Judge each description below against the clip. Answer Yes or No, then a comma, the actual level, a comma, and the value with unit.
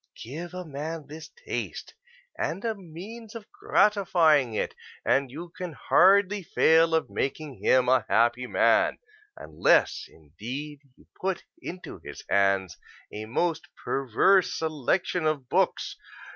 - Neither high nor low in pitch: Yes, medium, 160 Hz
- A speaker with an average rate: No, slow, 130 wpm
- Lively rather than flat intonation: Yes, wide, 5.9 semitones